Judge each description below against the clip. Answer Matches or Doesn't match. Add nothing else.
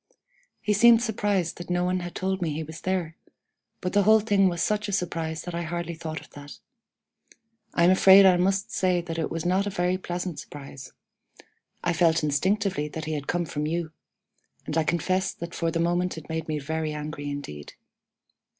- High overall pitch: Doesn't match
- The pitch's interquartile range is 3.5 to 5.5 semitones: Doesn't match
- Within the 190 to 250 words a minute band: Matches